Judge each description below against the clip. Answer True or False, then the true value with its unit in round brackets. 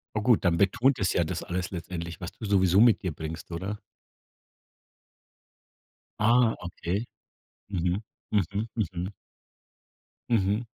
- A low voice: True (95 Hz)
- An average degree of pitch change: True (3.6 semitones)